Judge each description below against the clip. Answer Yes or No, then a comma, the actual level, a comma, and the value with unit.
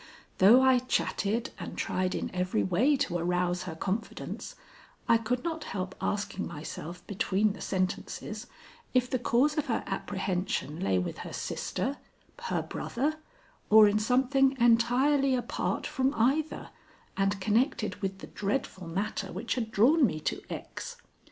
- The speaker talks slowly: No, average, 145 wpm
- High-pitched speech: Yes, high, 215 Hz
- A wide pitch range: Yes, wide, 5.7 semitones